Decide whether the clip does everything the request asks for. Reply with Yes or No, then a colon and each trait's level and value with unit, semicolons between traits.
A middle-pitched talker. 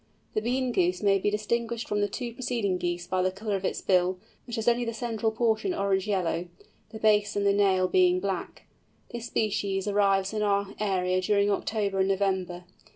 No: high, 200 Hz